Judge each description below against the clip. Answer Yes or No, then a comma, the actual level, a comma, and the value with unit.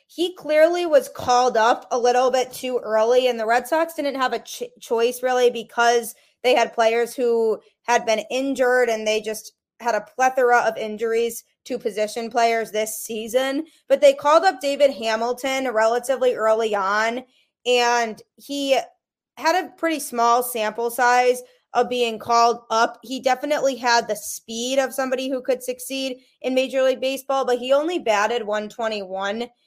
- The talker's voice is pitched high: Yes, high, 245 Hz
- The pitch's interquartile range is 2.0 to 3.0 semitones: Yes, average, 2.7 semitones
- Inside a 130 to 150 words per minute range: No, average, 165 wpm